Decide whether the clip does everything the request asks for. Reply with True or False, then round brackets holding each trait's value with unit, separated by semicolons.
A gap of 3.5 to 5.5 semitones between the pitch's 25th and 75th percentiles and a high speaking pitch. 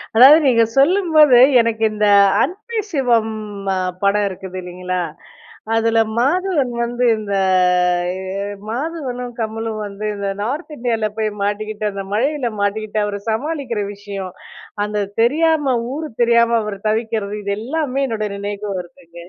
True (4.6 semitones; 225 Hz)